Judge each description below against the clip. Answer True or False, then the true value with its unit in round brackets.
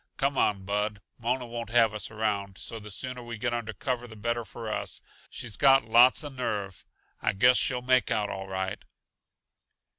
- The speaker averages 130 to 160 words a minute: False (185 wpm)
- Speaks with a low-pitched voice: True (115 Hz)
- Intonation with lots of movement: False (3.1 semitones)